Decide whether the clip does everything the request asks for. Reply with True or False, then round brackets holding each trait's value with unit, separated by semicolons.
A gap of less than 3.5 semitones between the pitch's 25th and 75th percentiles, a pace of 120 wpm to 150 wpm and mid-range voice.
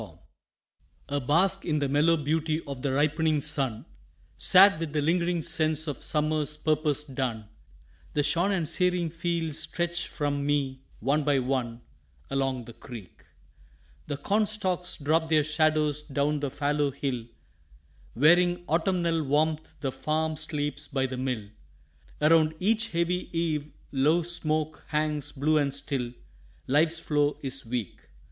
True (2.7 semitones; 140 wpm; 150 Hz)